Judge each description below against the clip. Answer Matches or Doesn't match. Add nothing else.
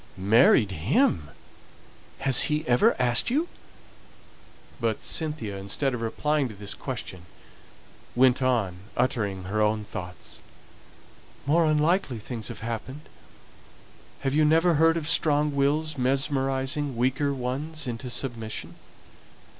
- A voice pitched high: Doesn't match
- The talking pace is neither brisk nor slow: Doesn't match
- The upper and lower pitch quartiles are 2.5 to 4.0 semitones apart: Doesn't match